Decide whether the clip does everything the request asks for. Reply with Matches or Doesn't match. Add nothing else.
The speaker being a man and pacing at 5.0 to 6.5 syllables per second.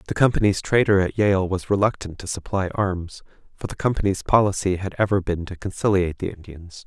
Matches